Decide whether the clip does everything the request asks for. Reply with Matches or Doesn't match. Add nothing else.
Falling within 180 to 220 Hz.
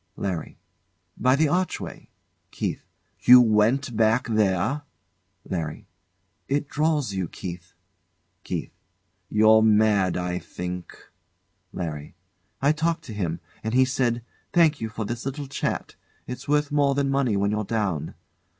Doesn't match